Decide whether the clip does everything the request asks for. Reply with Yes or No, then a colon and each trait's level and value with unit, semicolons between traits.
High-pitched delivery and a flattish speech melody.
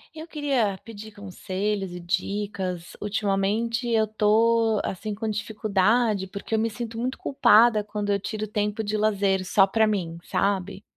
Yes: high, 210 Hz; narrow, 2.1 semitones